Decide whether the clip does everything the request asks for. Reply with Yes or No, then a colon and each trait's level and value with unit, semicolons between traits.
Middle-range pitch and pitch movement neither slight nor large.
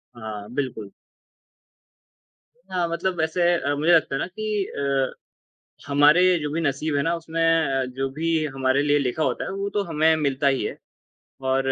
Yes: medium, 150 Hz; average, 3.5 semitones